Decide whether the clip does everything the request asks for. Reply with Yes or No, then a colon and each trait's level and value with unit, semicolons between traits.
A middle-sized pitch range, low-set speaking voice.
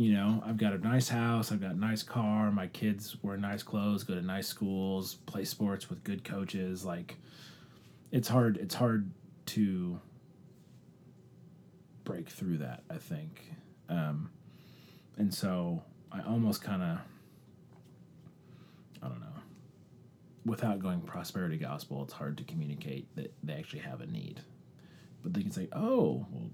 Yes: average, 3.5 semitones; low, 105 Hz